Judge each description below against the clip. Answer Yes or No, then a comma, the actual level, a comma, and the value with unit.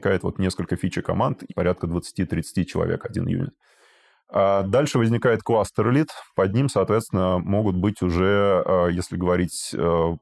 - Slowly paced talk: No, average, 125 wpm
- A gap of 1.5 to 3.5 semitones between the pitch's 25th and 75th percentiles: Yes, average, 2.9 semitones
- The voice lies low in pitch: Yes, very low, 95 Hz